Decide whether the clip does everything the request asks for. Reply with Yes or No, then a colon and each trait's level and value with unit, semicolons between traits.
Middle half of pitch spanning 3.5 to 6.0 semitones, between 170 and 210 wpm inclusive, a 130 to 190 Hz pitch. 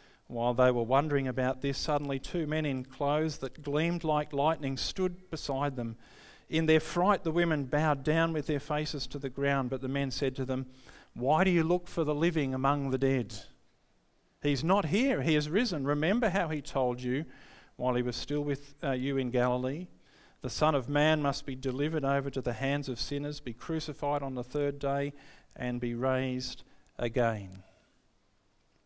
No: average, 2.9 semitones; average, 185 wpm; medium, 140 Hz